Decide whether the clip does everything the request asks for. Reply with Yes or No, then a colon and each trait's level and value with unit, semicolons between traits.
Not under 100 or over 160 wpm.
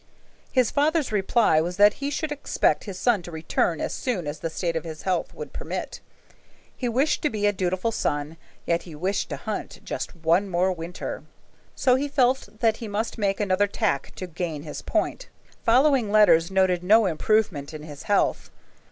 No: average, 185 wpm